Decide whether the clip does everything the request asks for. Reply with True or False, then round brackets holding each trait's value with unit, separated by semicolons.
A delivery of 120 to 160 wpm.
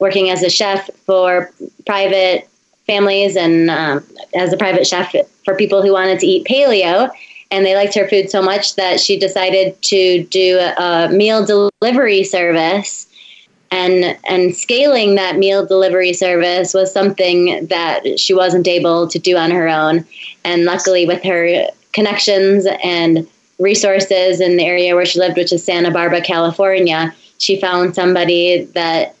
True (155 wpm)